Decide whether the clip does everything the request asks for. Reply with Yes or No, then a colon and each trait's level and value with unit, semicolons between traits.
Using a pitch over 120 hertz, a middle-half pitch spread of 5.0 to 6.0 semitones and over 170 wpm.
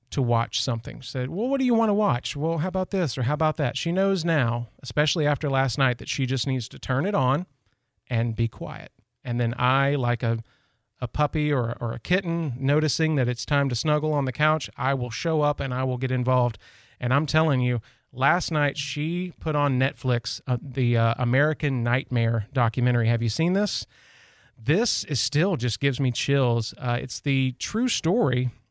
No: low, 135 Hz; average, 3.6 semitones; fast, 205 wpm